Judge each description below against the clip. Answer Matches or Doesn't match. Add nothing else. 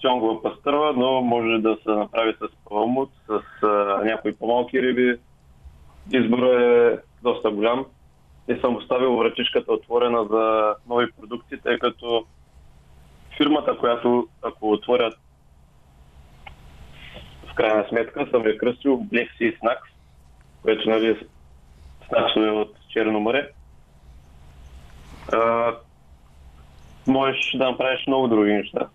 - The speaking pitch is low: Matches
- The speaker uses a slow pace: Matches